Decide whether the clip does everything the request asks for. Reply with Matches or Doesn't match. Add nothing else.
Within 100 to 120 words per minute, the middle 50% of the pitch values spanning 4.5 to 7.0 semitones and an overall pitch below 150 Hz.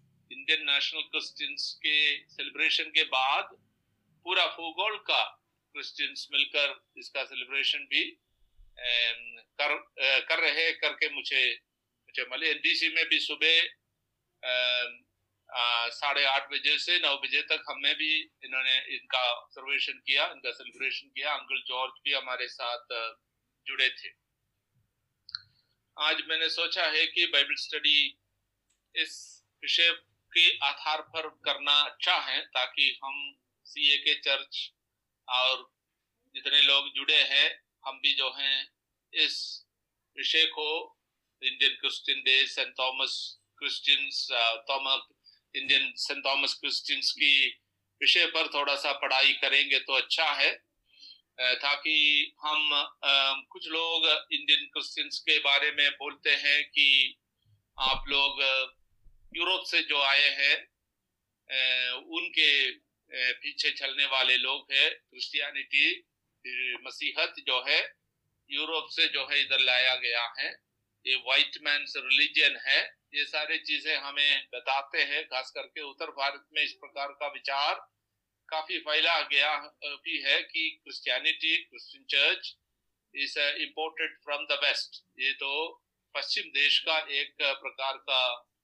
Doesn't match